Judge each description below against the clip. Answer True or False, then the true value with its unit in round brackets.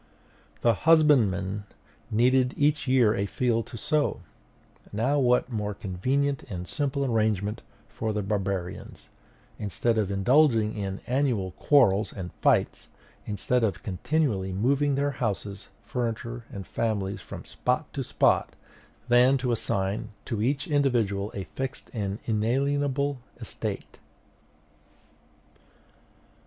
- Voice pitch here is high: False (115 Hz)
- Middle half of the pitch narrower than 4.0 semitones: False (5.0 semitones)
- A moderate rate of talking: False (115 wpm)